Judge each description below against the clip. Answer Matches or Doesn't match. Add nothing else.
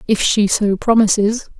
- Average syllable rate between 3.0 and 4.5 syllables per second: Matches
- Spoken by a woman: Matches